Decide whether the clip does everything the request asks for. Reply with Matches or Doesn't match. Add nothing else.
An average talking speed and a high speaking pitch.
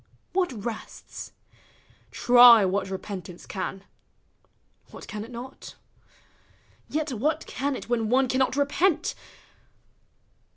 Doesn't match